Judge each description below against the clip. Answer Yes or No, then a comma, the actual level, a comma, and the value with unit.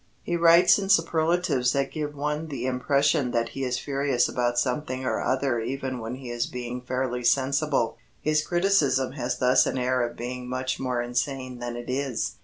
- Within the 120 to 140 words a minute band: No, average, 185 wpm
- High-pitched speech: No, low, 130 Hz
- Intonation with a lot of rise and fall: No, average, 2.7 semitones